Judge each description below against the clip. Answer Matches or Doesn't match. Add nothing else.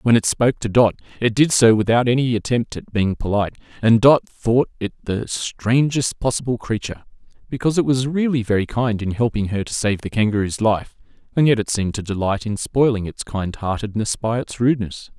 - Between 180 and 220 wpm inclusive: Matches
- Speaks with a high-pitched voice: Doesn't match